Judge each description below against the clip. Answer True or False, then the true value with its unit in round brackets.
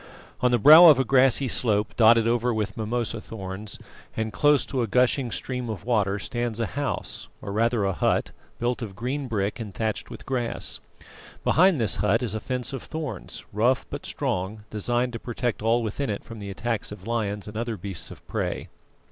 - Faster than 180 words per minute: True (195 wpm)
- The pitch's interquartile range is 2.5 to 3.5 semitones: True (3.1 semitones)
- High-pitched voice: False (115 Hz)